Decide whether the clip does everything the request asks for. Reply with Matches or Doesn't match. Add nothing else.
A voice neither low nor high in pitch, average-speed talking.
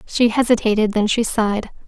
Doesn't match